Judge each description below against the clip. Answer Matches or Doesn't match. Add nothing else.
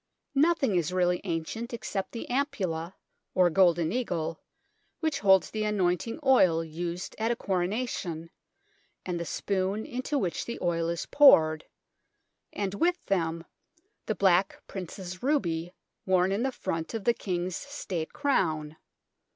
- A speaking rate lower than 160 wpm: Matches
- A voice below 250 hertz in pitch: Matches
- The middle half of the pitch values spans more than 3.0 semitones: Matches